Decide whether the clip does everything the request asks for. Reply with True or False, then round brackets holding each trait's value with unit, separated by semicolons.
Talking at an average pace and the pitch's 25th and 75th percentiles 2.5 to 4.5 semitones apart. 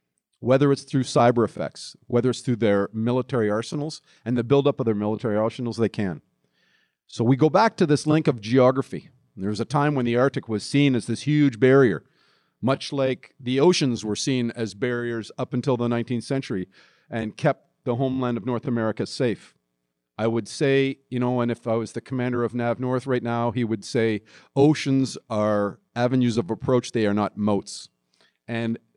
True (190 wpm; 3.1 semitones)